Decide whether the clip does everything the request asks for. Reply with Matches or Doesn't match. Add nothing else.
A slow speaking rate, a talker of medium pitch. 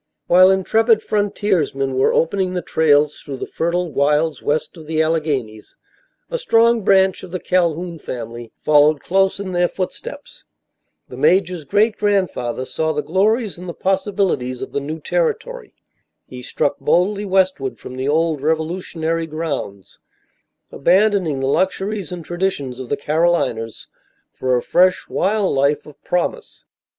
Doesn't match